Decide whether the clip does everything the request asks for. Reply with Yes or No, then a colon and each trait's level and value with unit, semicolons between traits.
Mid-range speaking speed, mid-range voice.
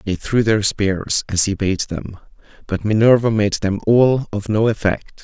No: average, 185 wpm; low, 105 Hz